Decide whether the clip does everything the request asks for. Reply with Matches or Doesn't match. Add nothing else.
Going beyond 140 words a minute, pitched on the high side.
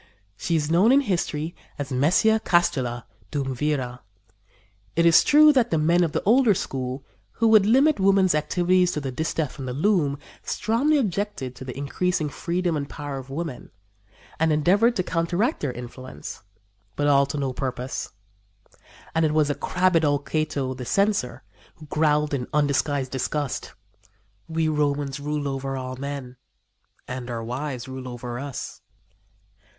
Doesn't match